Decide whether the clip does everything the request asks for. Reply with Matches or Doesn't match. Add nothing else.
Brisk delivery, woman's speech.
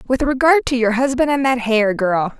Matches